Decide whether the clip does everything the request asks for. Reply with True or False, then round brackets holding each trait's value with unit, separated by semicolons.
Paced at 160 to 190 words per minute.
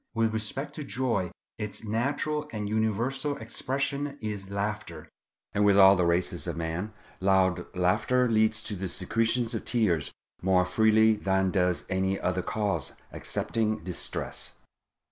False (140 wpm)